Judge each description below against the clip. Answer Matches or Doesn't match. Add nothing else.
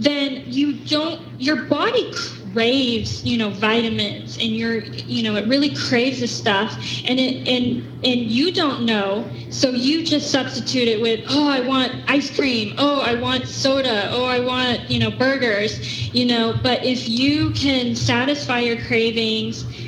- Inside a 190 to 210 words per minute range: Doesn't match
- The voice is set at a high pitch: Matches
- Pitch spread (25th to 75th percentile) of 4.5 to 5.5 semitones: Matches